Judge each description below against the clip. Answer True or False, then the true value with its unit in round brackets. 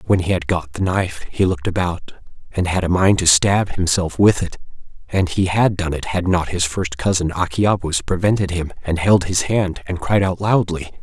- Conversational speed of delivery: False (210 wpm)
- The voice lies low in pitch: True (90 Hz)